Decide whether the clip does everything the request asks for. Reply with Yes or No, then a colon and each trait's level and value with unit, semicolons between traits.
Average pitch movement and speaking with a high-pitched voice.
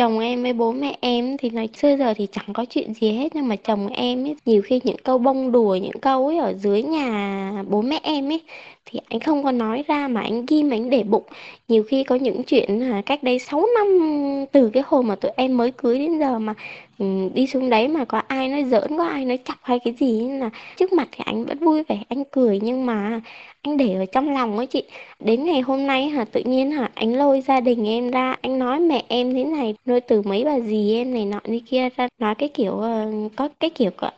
Yes: average, 3.7 semitones; very high, 250 Hz